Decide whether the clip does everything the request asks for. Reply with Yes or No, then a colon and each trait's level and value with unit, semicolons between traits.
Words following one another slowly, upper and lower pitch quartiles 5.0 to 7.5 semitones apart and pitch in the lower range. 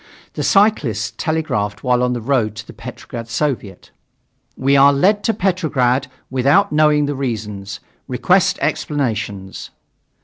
Yes: slow, 130 wpm; wide, 5.4 semitones; low, 130 Hz